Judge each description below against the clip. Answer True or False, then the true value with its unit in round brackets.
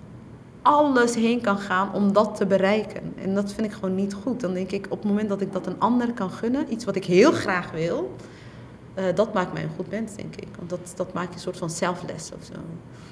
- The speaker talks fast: True (240 wpm)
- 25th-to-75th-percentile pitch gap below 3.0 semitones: True (2.4 semitones)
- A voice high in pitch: True (195 Hz)